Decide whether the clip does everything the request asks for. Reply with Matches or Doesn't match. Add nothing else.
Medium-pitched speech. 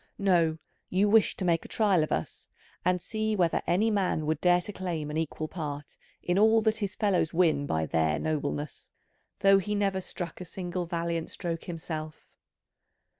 Matches